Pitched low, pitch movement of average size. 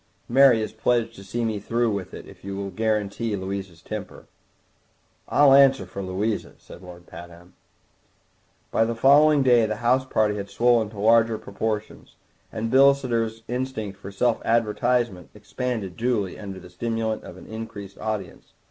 Yes: low, 110 Hz; average, 3.3 semitones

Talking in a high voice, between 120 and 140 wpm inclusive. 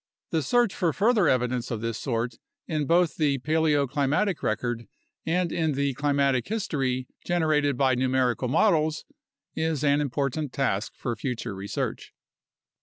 No: medium, 140 Hz; slow, 135 wpm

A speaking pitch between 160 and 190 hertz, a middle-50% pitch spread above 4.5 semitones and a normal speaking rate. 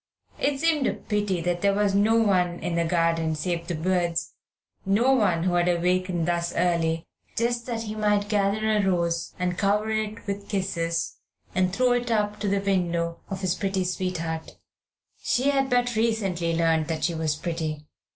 No: medium, 185 Hz; average, 3.9 semitones; average, 180 wpm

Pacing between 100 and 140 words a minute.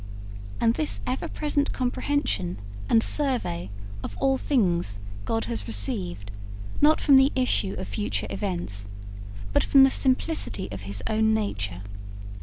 Yes: slow, 135 wpm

